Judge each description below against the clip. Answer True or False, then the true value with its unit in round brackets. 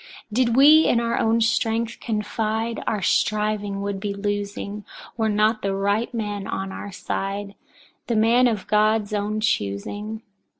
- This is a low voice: False (215 Hz)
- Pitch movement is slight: True (1.9 semitones)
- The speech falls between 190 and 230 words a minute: False (155 wpm)